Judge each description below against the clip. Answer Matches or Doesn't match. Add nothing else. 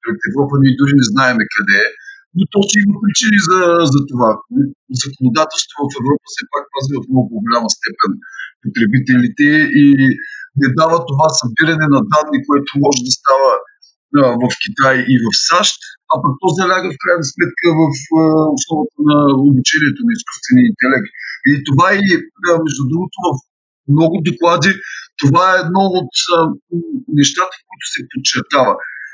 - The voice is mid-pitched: Matches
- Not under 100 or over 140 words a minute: Doesn't match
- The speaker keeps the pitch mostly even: Doesn't match